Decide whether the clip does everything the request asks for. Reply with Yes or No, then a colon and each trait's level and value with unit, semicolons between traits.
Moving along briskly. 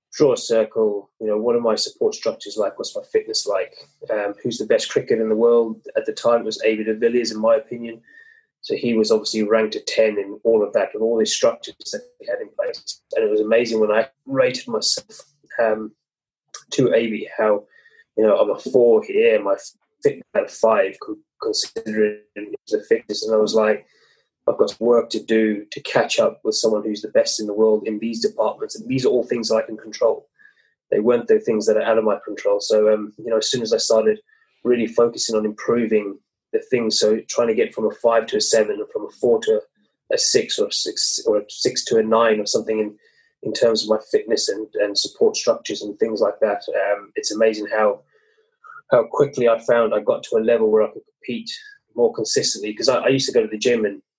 Yes: fast, 230 wpm